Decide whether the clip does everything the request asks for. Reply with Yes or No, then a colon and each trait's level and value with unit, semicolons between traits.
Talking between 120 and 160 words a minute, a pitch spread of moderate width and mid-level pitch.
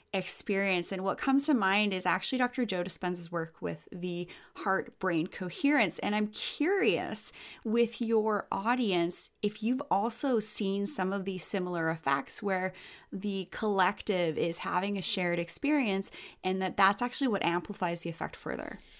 No: average, 155 wpm; average, 3.8 semitones; high, 195 Hz